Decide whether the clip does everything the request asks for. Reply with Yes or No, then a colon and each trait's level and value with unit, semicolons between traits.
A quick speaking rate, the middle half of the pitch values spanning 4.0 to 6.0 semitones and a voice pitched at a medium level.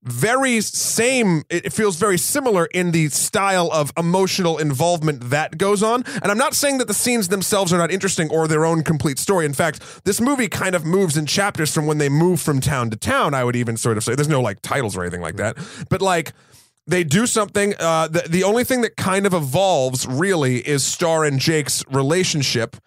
Yes: fast, 215 wpm; average, 5.2 semitones; medium, 165 Hz